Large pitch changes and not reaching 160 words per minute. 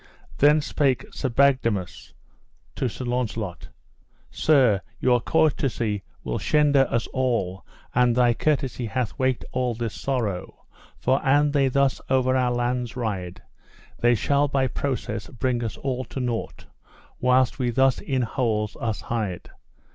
No: narrow, 2.6 semitones; average, 140 wpm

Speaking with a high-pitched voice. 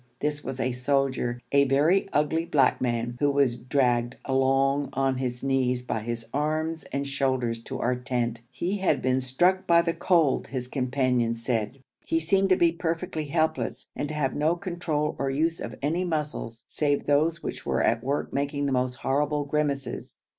No: medium, 140 Hz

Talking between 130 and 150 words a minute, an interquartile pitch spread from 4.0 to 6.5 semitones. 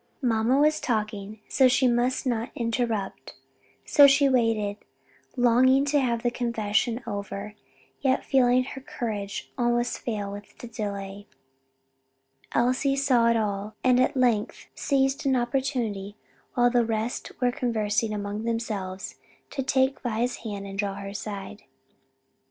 No: average, 140 wpm; average, 3.5 semitones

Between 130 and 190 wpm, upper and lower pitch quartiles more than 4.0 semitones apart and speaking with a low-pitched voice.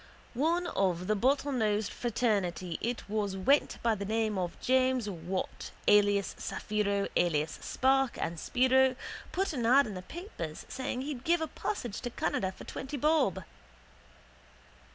No: average, 145 wpm; average, 5.1 semitones; high, 225 Hz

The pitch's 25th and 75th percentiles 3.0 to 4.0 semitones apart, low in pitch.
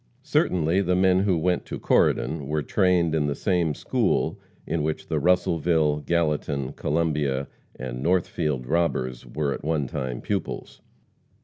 Yes: average, 3.3 semitones; very low, 80 Hz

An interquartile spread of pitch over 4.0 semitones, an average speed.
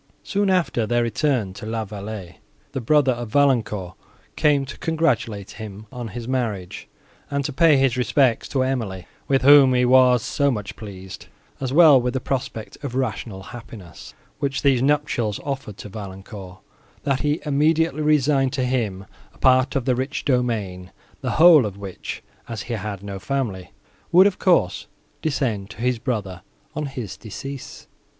Yes: average, 4.9 semitones; average, 165 wpm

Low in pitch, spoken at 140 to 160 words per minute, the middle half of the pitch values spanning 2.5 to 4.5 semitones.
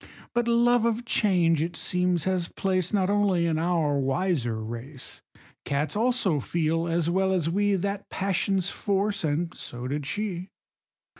No: medium, 180 Hz; average, 150 wpm; average, 4.1 semitones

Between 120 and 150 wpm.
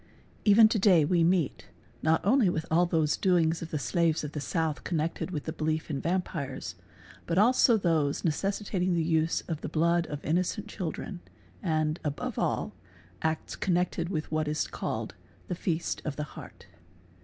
No: average, 175 wpm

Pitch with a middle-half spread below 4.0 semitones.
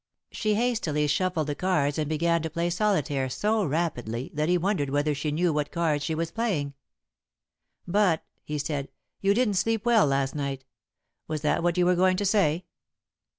No: average, 4.3 semitones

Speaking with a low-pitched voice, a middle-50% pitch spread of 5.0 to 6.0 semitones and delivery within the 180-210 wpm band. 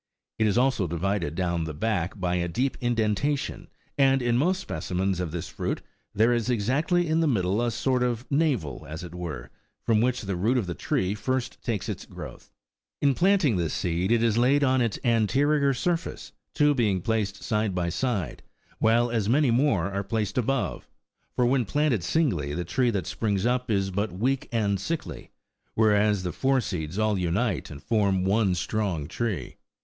Yes: low, 110 Hz; wide, 5.6 semitones; average, 185 wpm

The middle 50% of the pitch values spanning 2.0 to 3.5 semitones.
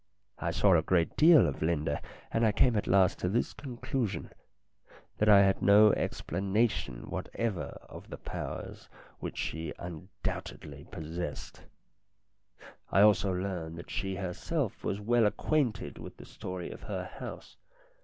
No: average, 4.1 semitones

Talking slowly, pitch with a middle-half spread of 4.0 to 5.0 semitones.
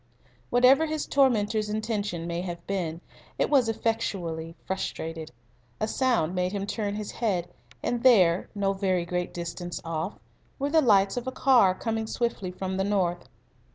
No: average, 160 wpm; average, 4.6 semitones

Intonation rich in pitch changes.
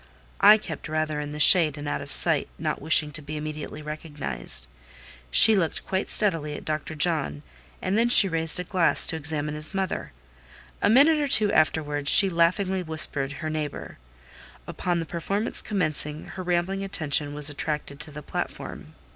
No: average, 3.8 semitones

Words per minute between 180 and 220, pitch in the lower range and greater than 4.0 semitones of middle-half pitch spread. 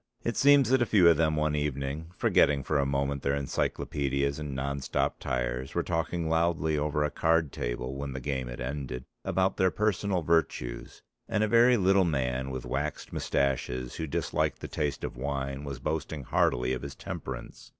No: average, 185 wpm; very low, 70 Hz; average, 3.6 semitones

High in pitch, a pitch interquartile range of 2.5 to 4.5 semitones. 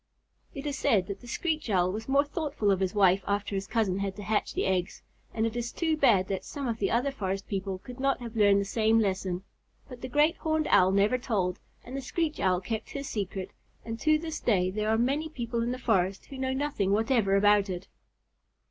No: high, 220 Hz; average, 5.2 semitones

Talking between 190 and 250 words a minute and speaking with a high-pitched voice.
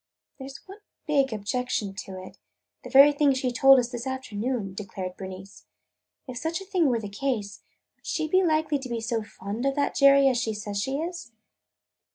Yes: average, 200 wpm; very high, 255 Hz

